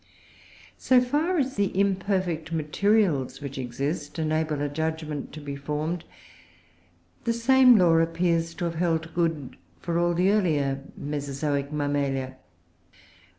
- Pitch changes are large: No, average, 4.2 semitones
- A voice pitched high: No, medium, 160 Hz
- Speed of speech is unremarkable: No, slow, 125 wpm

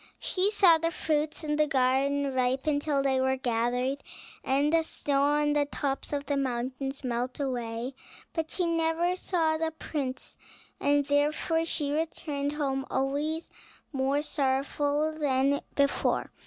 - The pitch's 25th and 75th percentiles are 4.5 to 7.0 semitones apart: No, average, 2.7 semitones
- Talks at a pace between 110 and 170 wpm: Yes, average, 140 wpm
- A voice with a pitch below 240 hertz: No, very high, 285 Hz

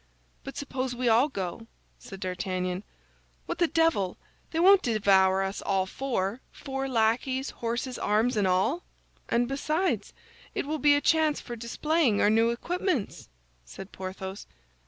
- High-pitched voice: Yes, high, 235 Hz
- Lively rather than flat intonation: Yes, wide, 6.5 semitones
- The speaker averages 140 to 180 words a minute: Yes, average, 145 wpm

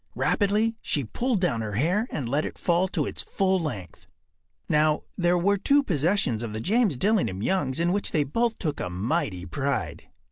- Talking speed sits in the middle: Yes, average, 185 wpm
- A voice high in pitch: No, medium, 165 Hz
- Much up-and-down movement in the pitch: Yes, wide, 7.5 semitones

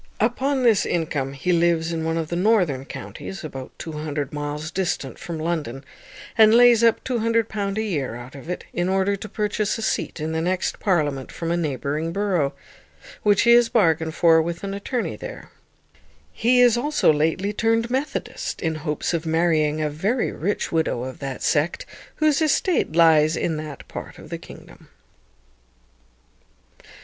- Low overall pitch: No, medium, 170 Hz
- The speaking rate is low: No, average, 165 wpm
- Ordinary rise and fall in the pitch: No, wide, 5.9 semitones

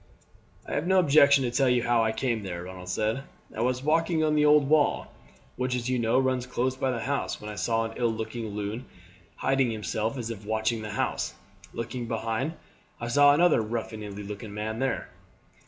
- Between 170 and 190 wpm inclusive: No, average, 200 wpm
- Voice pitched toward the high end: No, low, 120 Hz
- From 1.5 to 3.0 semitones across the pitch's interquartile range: No, average, 3.5 semitones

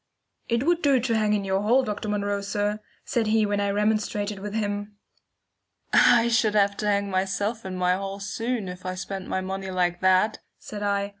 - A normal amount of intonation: No, narrow, 1.8 semitones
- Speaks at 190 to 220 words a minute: Yes, average, 200 wpm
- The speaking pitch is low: No, high, 205 Hz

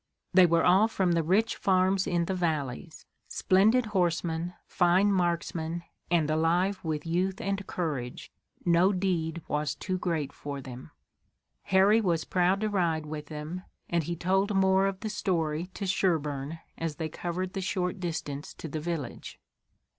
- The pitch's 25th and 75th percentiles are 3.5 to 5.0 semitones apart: No, average, 3.0 semitones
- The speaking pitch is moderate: Yes, medium, 175 Hz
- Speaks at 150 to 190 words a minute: Yes, average, 155 wpm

